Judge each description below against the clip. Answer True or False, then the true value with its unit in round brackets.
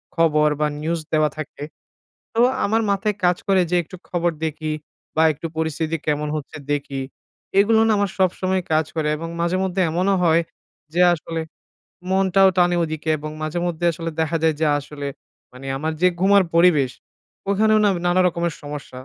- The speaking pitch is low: False (165 Hz)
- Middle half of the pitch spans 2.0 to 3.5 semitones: True (3.2 semitones)